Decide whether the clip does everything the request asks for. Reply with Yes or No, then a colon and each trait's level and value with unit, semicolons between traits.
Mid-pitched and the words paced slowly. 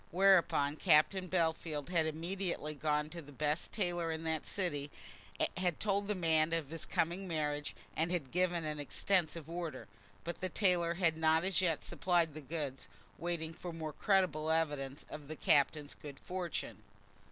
No: medium, 165 Hz; average, 165 wpm